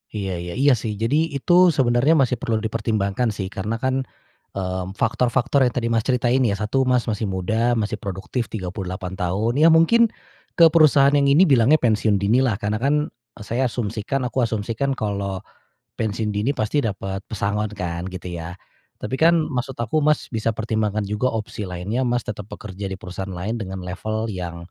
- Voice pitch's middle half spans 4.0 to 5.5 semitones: Yes, average, 4.7 semitones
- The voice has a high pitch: No, low, 110 Hz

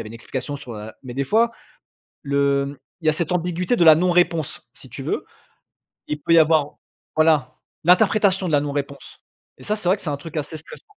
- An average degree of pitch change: Yes, average, 3.9 semitones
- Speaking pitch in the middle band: Yes, medium, 155 Hz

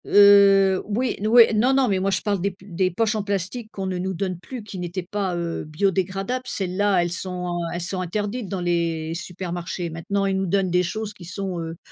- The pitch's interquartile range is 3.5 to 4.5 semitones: No, narrow, 2.5 semitones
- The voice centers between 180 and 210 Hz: Yes, high, 190 Hz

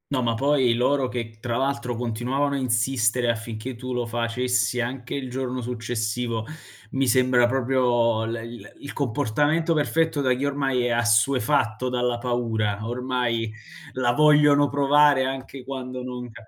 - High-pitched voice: No, low, 125 Hz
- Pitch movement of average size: No, narrow, 2.3 semitones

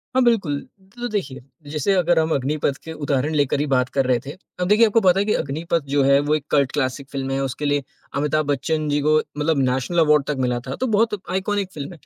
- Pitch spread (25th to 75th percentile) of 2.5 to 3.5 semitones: No, average, 4.3 semitones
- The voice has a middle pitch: Yes, medium, 150 Hz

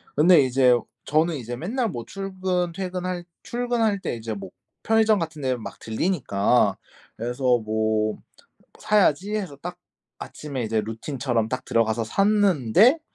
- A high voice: No, medium, 150 Hz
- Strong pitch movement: Yes, wide, 8.6 semitones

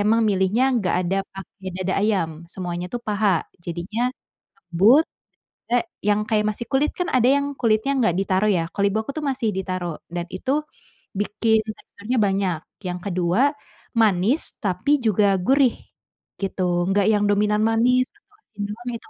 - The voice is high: Yes, high, 205 Hz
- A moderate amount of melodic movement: Yes, average, 3.5 semitones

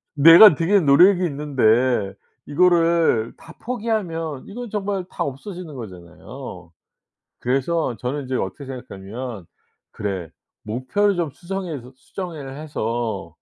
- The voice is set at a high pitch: No, medium, 140 Hz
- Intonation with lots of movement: Yes, wide, 6.7 semitones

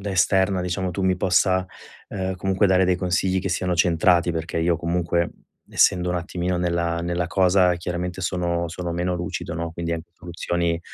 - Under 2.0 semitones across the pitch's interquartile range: Yes, narrow, 1.4 semitones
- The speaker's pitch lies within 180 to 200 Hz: No, very low, 90 Hz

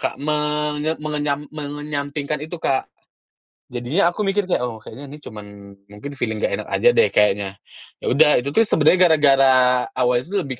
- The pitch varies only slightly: No, average, 3.1 semitones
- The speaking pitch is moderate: Yes, medium, 145 Hz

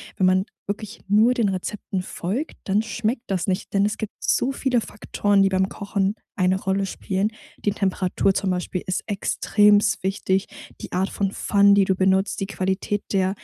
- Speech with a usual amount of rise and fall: No, narrow, 1.6 semitones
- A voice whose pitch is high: Yes, high, 195 Hz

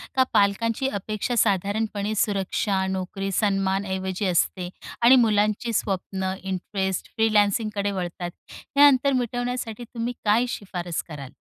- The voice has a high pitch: Yes, high, 205 Hz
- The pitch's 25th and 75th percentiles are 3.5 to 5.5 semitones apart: No, average, 3.0 semitones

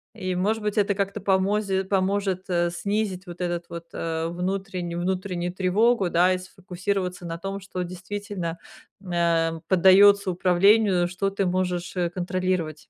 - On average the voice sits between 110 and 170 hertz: No, medium, 185 Hz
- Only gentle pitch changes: Yes, narrow, 2.1 semitones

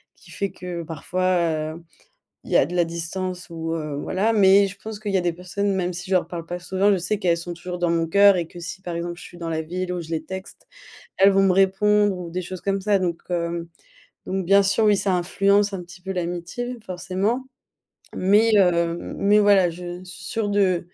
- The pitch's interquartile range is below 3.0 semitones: Yes, narrow, 2.4 semitones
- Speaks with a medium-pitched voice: Yes, medium, 180 Hz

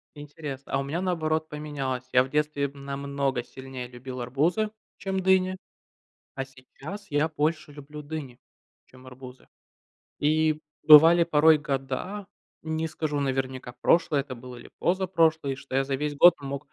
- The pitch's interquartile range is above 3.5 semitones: No, average, 2.9 semitones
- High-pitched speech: No, medium, 145 Hz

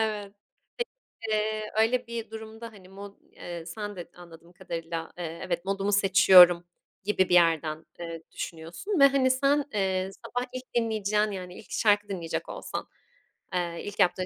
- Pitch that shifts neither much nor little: Yes, average, 3.9 semitones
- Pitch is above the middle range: Yes, high, 195 Hz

